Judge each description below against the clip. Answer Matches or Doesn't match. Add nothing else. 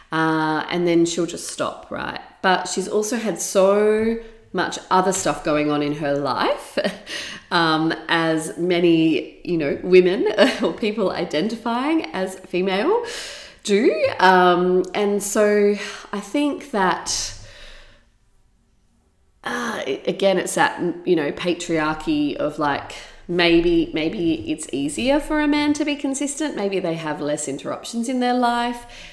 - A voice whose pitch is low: Doesn't match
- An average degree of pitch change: Doesn't match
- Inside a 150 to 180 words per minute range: Doesn't match